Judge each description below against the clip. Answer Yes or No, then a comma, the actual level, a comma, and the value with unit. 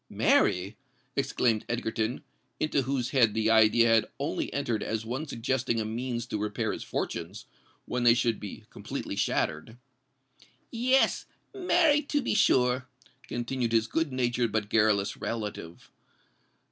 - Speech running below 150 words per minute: Yes, slow, 135 wpm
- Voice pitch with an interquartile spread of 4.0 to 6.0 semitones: No, average, 2.9 semitones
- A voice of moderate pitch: No, low, 115 Hz